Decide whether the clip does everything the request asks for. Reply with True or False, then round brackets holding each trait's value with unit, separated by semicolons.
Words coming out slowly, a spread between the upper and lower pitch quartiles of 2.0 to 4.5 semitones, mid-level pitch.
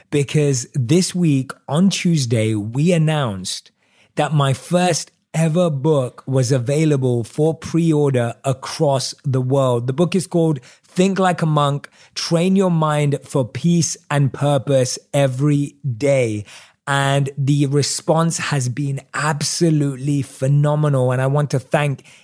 True (130 wpm; 3.3 semitones; 145 Hz)